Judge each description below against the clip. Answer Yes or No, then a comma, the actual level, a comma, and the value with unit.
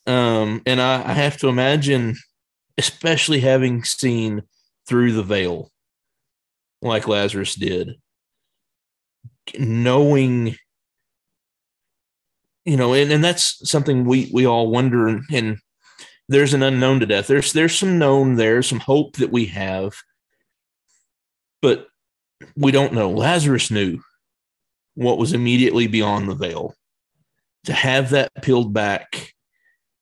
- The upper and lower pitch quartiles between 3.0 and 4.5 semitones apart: Yes, average, 4.0 semitones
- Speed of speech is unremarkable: No, slow, 120 wpm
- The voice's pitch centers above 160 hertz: No, low, 125 Hz